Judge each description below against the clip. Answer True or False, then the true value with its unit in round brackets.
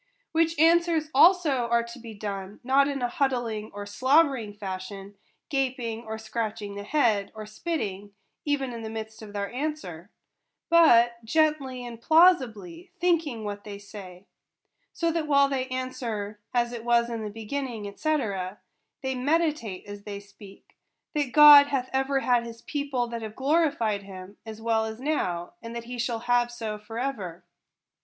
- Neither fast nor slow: True (170 wpm)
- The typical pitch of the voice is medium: False (235 Hz)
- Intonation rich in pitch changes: False (4.9 semitones)